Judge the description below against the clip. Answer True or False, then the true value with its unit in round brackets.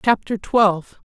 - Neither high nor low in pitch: False (205 Hz)